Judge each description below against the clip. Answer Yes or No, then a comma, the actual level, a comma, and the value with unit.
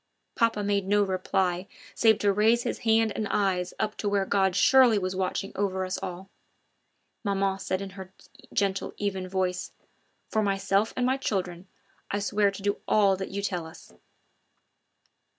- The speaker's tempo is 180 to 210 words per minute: No, average, 165 wpm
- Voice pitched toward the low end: No, high, 195 Hz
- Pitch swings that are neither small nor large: No, narrow, 1.6 semitones